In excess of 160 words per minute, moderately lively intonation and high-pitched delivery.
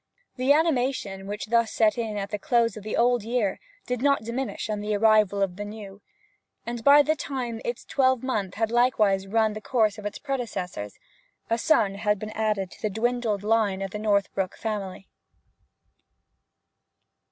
Yes: average, 175 wpm; average, 3.0 semitones; high, 215 Hz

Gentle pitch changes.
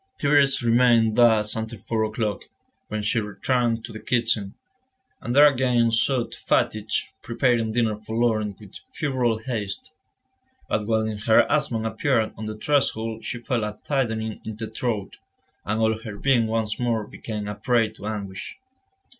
Yes: narrow, 2.0 semitones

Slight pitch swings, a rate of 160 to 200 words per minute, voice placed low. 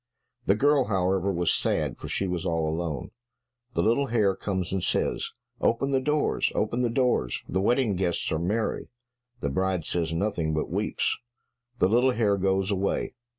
No: average, 5.1 semitones; average, 170 wpm; very low, 95 Hz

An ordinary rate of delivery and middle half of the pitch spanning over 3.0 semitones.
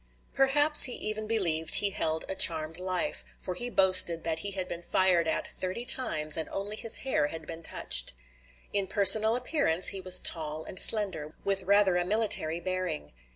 Yes: average, 180 wpm; average, 4.4 semitones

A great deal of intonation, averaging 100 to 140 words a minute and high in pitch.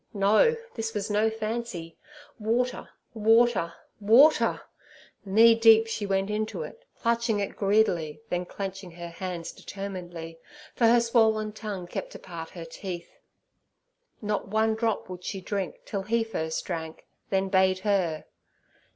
No: average, 3.6 semitones; slow, 135 wpm; high, 205 Hz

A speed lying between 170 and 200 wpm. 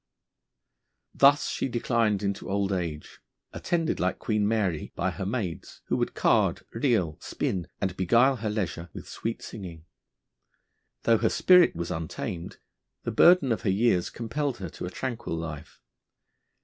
No: average, 150 wpm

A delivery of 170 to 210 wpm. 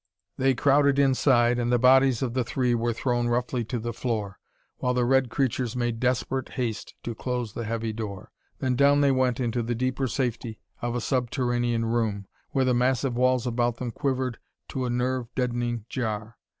Yes: average, 185 wpm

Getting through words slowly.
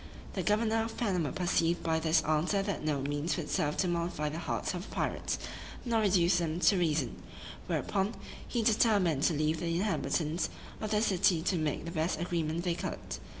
No: average, 190 wpm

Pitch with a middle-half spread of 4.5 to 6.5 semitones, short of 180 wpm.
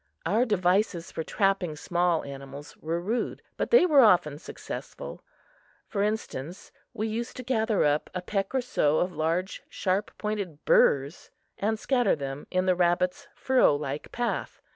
Yes: wide, 5.5 semitones; average, 155 wpm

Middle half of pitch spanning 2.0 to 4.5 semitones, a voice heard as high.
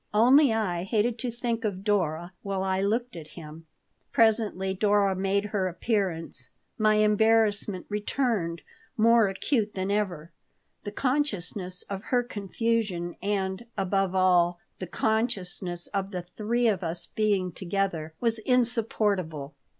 Yes: average, 3.4 semitones; high, 200 Hz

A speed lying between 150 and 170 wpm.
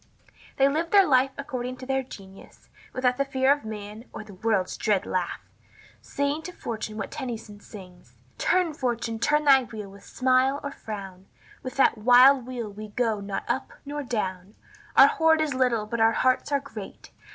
No: average, 185 wpm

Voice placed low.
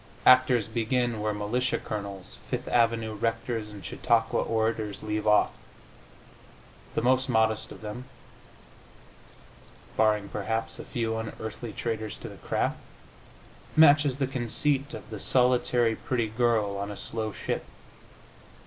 Yes: low, 115 Hz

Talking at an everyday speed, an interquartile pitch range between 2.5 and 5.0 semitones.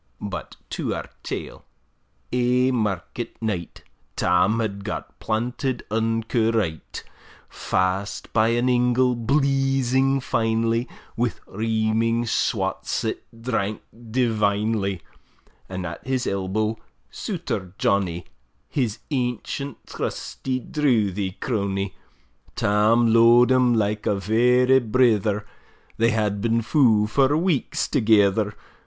No: slow, 105 wpm; average, 3.2 semitones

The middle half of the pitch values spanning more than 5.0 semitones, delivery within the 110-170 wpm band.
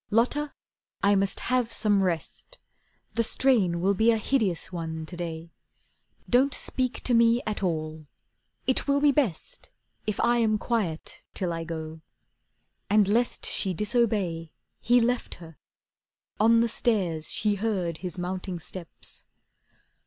Yes: wide, 5.4 semitones; average, 140 wpm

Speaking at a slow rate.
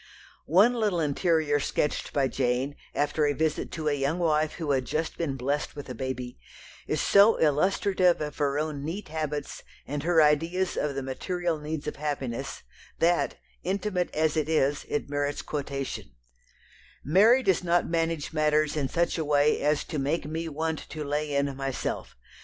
No: average, 170 wpm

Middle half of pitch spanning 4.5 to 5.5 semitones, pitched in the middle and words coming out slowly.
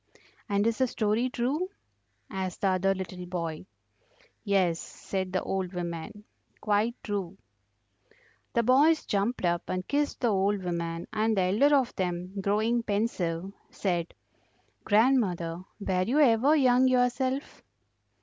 No: average, 4.8 semitones; high, 200 Hz; slow, 130 wpm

